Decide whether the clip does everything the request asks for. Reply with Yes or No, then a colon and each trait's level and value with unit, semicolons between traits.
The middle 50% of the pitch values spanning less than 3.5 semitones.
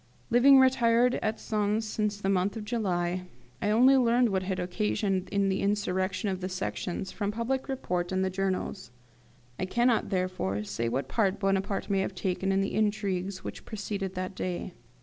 Yes: average, 2.7 semitones